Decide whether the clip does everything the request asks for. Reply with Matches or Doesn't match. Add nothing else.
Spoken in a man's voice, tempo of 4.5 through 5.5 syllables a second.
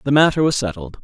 Doesn't match